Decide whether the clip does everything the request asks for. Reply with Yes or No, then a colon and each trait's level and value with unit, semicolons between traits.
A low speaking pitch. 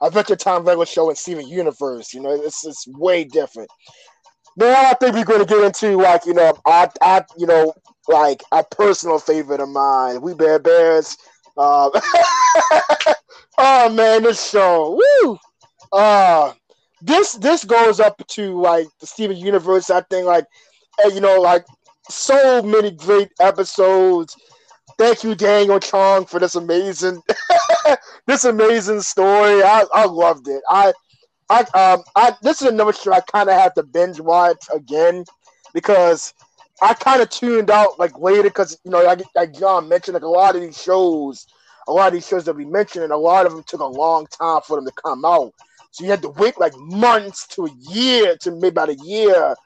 No: high, 190 Hz